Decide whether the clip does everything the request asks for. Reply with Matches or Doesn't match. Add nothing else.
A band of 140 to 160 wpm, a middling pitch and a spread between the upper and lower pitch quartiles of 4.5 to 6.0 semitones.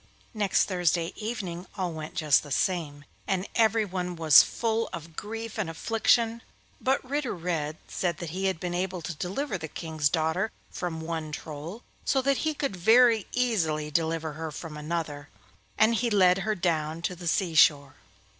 Doesn't match